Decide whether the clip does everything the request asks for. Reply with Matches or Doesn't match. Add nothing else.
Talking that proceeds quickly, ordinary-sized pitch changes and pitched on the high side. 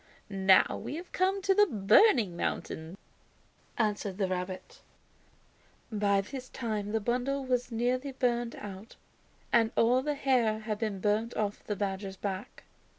Doesn't match